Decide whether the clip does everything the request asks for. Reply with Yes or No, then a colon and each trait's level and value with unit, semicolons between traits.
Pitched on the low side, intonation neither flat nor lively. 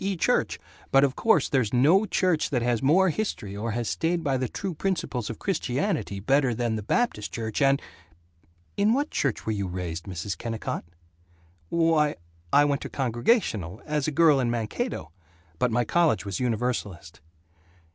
No: low, 130 Hz; wide, 6.9 semitones